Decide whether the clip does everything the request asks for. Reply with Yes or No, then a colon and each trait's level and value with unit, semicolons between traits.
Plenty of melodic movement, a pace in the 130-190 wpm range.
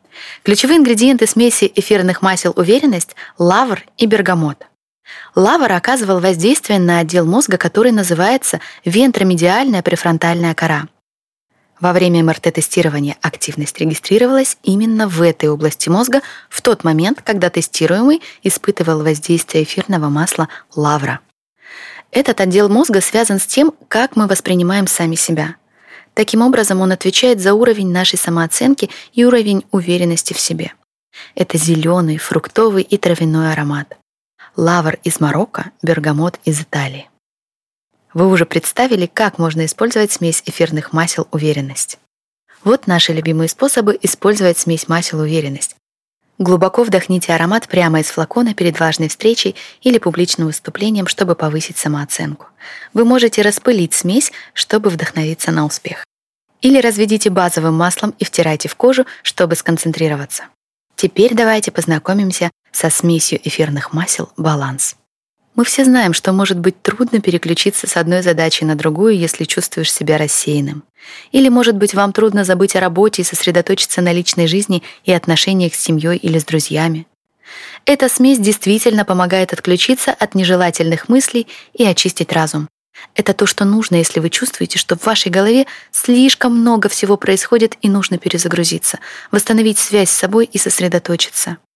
No: average, 4.7 semitones; average, 135 wpm